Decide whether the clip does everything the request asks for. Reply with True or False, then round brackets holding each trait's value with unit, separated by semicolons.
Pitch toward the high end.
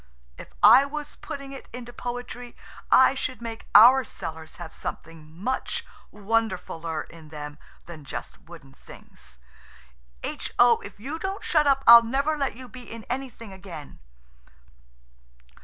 True (230 Hz)